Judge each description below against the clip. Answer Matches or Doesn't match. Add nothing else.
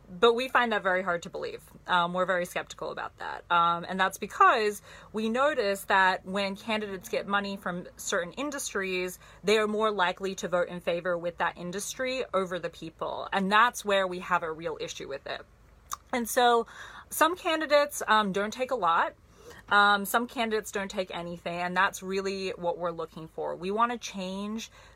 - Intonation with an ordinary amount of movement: Matches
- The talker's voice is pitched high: Matches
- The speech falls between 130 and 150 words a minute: Doesn't match